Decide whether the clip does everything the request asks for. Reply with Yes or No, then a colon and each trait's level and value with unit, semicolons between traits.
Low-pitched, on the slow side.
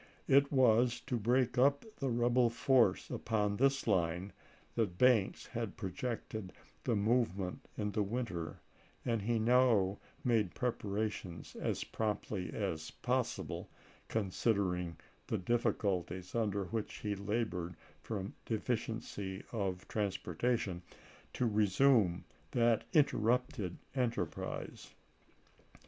Yes: low, 110 Hz; slow, 110 wpm